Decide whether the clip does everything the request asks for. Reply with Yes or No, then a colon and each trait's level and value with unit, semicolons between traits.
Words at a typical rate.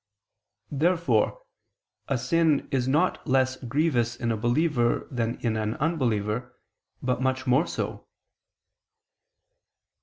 No: slow, 110 wpm